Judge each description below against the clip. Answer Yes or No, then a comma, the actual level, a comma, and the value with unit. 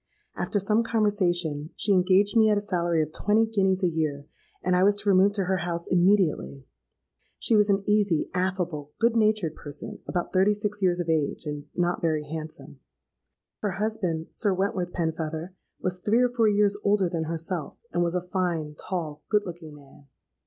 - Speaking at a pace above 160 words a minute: Yes, average, 180 wpm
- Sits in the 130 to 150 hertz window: No, medium, 180 Hz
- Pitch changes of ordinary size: Yes, average, 4.0 semitones